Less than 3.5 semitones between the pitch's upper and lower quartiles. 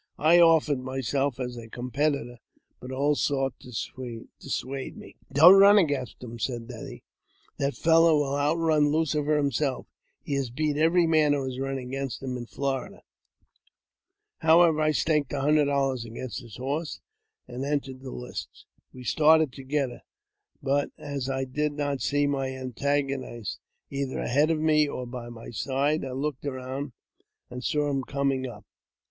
Yes: narrow, 2.6 semitones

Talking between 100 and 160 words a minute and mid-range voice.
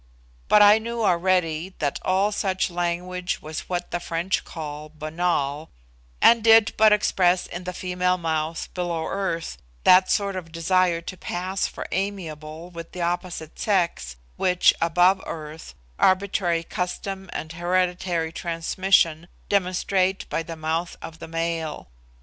Yes: average, 140 wpm; medium, 175 Hz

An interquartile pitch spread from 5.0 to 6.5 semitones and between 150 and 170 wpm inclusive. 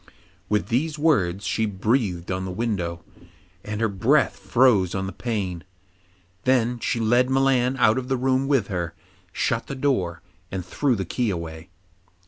Yes: wide, 5.6 semitones; average, 160 wpm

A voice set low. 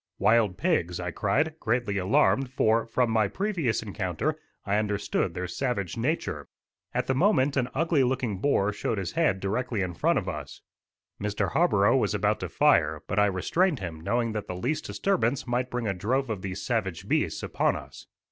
Yes: low, 115 Hz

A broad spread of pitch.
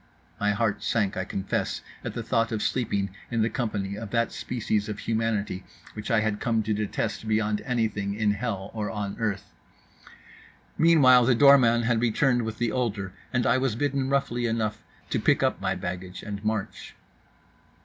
No: narrow, 2.6 semitones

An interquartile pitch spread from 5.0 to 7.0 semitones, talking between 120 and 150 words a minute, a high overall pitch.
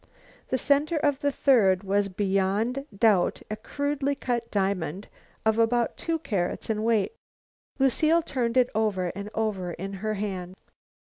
Yes: average, 5.3 semitones; average, 140 wpm; high, 220 Hz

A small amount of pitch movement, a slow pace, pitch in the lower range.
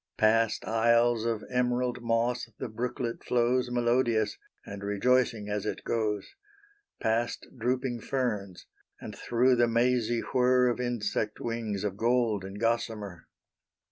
Yes: narrow, 2.3 semitones; slow, 125 wpm; low, 115 Hz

